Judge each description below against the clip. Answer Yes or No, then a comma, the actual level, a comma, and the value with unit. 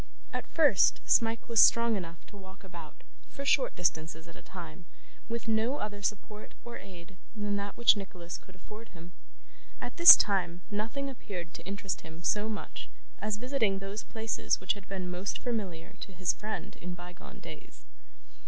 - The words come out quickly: No, average, 170 wpm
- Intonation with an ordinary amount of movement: Yes, average, 3.7 semitones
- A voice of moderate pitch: No, high, 200 Hz